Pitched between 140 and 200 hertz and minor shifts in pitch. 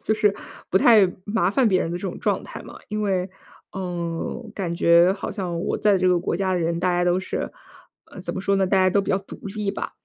Yes: medium, 185 Hz; narrow, 2.1 semitones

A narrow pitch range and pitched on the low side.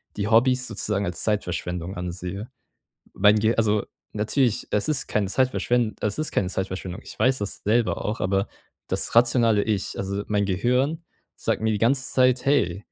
No: average, 3.9 semitones; low, 105 Hz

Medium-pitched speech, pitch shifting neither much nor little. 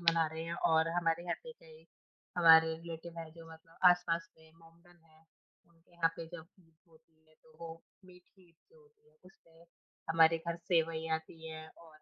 No: medium, 165 Hz; narrow, 1.1 semitones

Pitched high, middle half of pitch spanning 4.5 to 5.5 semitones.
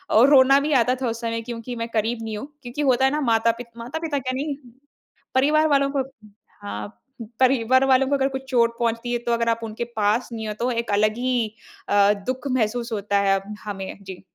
No: high, 235 Hz; average, 3.0 semitones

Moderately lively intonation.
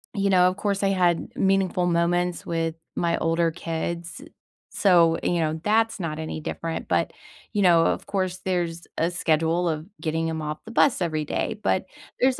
No: narrow, 2.3 semitones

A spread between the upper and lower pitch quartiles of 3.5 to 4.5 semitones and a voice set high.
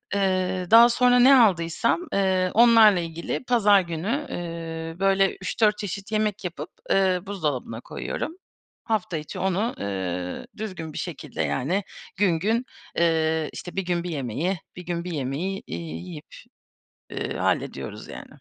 No: average, 4.1 semitones; medium, 180 Hz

